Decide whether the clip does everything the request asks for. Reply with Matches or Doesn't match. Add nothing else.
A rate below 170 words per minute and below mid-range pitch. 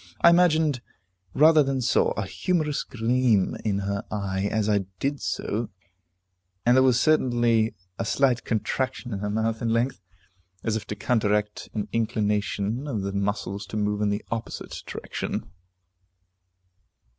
Matches